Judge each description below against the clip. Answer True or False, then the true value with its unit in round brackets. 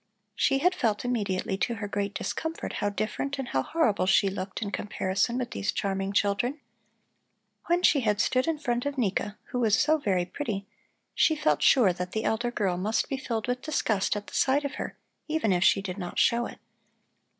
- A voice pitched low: False (220 Hz)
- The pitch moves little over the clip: False (5.1 semitones)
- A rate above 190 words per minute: True (200 wpm)